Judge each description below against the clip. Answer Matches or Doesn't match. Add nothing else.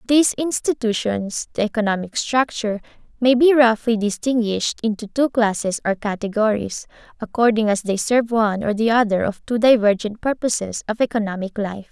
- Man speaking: Doesn't match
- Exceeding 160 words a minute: Doesn't match